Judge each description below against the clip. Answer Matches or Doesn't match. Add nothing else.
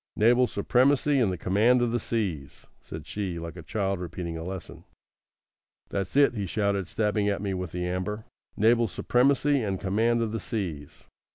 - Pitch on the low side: Matches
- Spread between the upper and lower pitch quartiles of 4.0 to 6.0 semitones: Matches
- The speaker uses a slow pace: Doesn't match